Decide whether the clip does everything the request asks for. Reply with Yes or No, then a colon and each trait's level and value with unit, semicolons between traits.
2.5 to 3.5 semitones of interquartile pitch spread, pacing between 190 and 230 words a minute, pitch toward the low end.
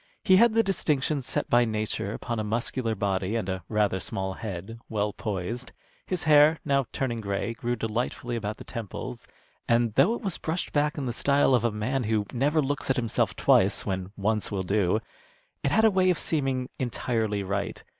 No: average, 5.0 semitones; average, 195 wpm; low, 115 Hz